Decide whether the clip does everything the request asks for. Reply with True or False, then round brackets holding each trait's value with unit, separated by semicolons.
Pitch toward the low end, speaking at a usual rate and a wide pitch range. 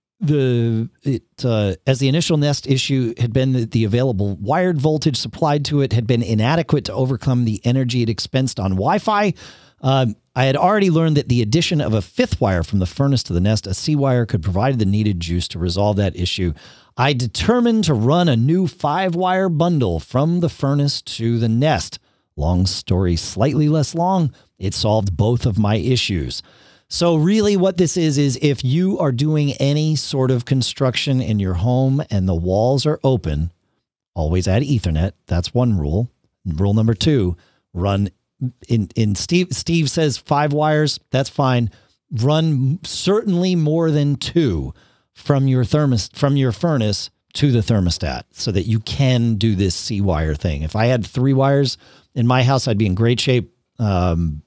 True (125 Hz; 180 wpm; 6.2 semitones)